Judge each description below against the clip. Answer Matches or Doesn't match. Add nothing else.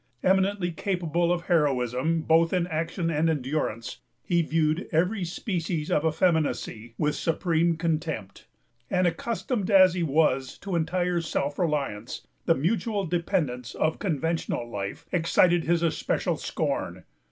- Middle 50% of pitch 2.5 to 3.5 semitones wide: Matches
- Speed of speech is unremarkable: Doesn't match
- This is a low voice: Doesn't match